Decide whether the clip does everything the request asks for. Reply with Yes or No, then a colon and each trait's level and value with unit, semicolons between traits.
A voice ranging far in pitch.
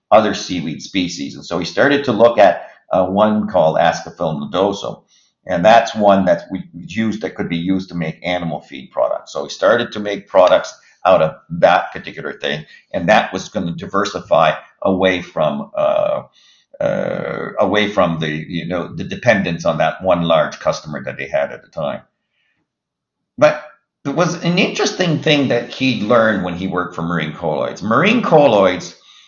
Yes: wide, 8.1 semitones